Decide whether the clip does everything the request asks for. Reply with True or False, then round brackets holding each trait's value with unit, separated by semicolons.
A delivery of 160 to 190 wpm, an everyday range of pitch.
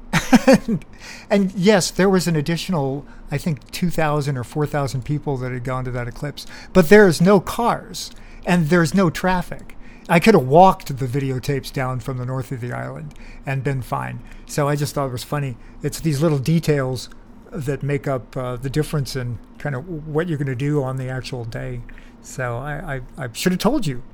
False (200 wpm; 4.8 semitones)